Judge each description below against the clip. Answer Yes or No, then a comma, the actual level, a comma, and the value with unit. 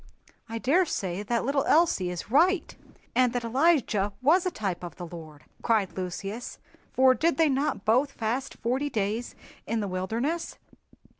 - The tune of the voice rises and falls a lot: Yes, wide, 6.4 semitones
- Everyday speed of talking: Yes, average, 155 wpm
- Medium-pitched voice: No, high, 235 Hz